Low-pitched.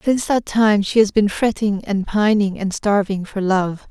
No: high, 205 Hz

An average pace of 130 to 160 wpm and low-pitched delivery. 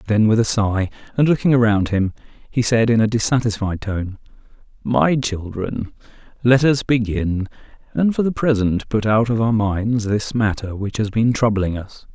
No: average, 175 wpm; low, 110 Hz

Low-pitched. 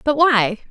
No: very high, 260 Hz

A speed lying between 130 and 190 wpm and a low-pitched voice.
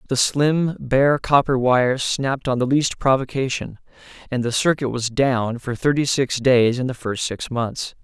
Yes: average, 180 wpm; low, 130 Hz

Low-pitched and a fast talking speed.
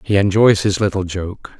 No: very low, 95 Hz; average, 190 wpm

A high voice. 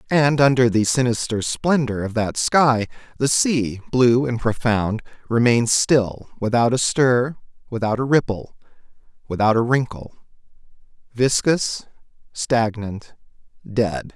No: low, 120 Hz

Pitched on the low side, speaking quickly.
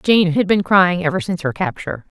No: medium, 185 Hz; fast, 220 wpm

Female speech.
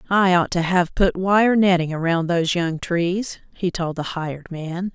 Yes: female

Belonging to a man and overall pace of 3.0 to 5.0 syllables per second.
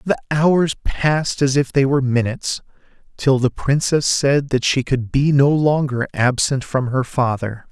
Yes: male; 4.3 syllables/s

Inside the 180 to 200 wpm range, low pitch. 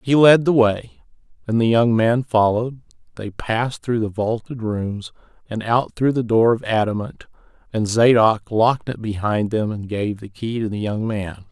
Yes: average, 190 wpm; low, 110 Hz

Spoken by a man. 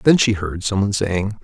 Yes: male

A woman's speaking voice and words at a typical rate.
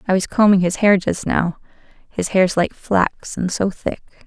Yes: female; average, 195 wpm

